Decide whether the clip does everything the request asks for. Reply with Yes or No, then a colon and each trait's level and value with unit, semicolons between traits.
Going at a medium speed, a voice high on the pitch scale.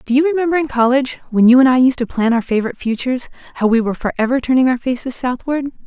No: fast, 235 wpm; very high, 255 Hz